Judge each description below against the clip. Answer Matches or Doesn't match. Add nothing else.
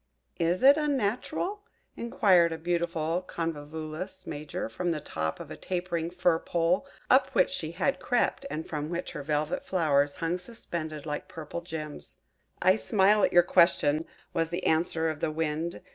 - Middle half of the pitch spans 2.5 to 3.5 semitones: Matches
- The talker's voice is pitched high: Doesn't match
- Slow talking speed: Doesn't match